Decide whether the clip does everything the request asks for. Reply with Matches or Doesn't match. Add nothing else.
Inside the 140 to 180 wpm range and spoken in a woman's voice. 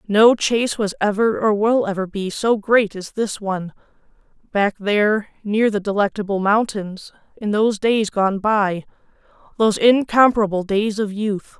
Matches